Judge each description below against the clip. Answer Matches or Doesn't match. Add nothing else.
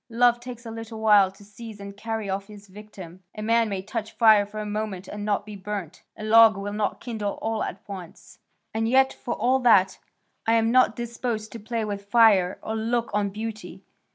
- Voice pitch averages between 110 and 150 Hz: Doesn't match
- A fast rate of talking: Matches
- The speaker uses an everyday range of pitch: Doesn't match